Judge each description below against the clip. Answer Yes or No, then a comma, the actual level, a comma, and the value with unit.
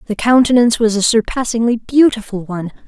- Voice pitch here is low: No, high, 225 Hz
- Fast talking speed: No, average, 145 wpm